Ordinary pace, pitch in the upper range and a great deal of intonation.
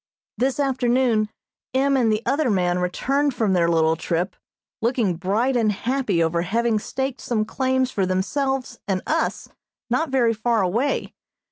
Yes: average, 150 wpm; high, 230 Hz; wide, 5.8 semitones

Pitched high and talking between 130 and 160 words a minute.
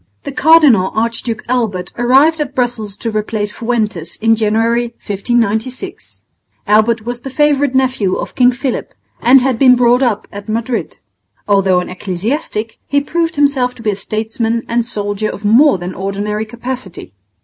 Yes: high, 230 Hz; average, 155 wpm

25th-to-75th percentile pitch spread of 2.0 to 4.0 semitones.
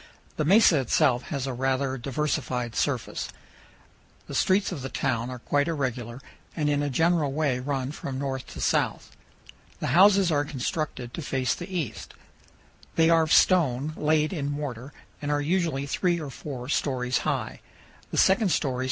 Yes: average, 3.4 semitones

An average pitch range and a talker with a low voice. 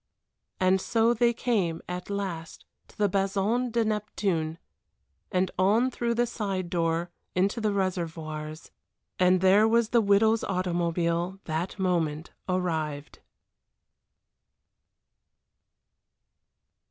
No: average, 4.0 semitones; medium, 185 Hz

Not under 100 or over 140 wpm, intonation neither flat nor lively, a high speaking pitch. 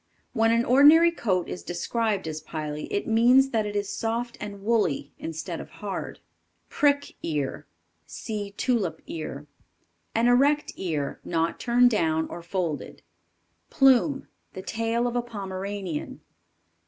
No: slow, 135 wpm; wide, 6.0 semitones; high, 210 Hz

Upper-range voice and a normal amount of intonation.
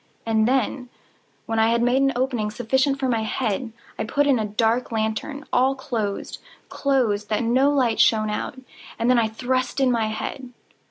Yes: high, 240 Hz; average, 3.1 semitones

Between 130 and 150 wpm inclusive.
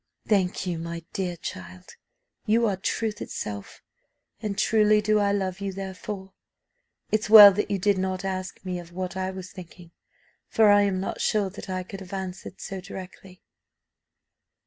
No: average, 170 wpm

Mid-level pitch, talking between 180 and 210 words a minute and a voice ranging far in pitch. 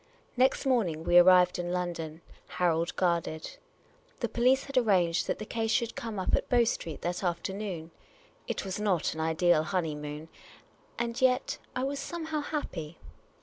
No: medium, 180 Hz; average, 155 wpm; wide, 6.1 semitones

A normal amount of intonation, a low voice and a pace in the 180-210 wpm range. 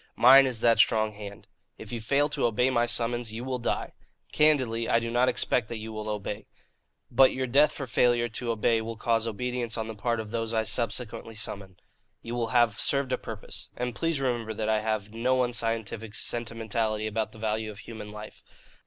No: narrow, 2.1 semitones; low, 115 Hz; average, 200 wpm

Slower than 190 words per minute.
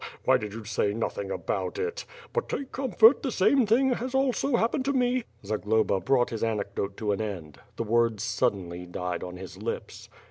No: average, 200 wpm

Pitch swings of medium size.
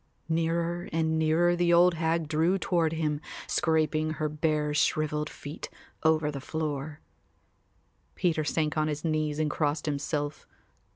No: narrow, 1.4 semitones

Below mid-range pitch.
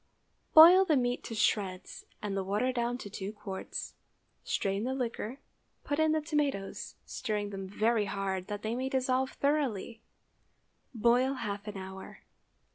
No: high, 225 Hz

